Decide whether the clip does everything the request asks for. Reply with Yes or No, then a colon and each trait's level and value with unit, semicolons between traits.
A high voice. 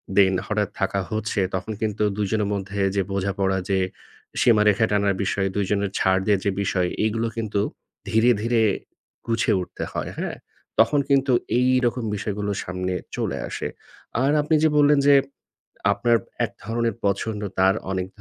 No: low, 105 Hz